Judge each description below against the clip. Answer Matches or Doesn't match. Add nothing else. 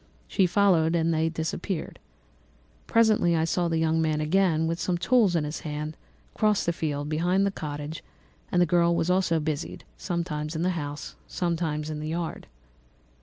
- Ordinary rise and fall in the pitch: Doesn't match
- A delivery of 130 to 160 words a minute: Doesn't match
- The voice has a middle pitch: Matches